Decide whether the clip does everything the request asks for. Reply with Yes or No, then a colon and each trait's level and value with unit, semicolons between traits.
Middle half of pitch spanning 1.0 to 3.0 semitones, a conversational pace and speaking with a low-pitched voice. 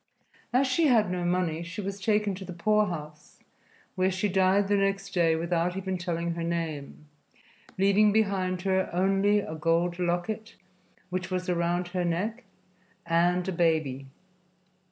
No: narrow, 2.5 semitones; average, 150 wpm; medium, 180 Hz